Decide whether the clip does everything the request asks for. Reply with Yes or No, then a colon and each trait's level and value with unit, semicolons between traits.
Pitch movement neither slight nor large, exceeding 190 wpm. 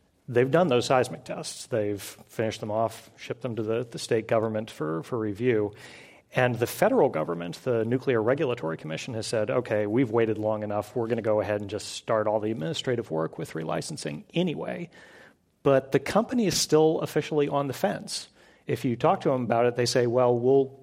Yes: average, 3.9 semitones; average, 200 wpm